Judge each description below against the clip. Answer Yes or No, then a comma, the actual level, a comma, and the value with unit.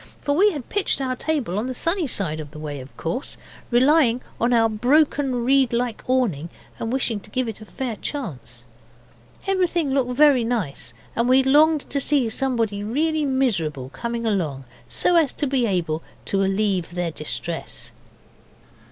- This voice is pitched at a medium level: No, high, 240 Hz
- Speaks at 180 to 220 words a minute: No, average, 170 wpm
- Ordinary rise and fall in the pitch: No, wide, 6.3 semitones